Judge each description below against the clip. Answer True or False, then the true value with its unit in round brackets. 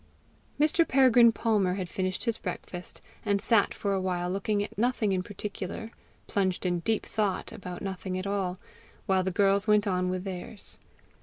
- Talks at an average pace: True (170 wpm)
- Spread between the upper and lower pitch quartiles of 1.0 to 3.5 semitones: True (2.4 semitones)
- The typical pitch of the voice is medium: False (195 Hz)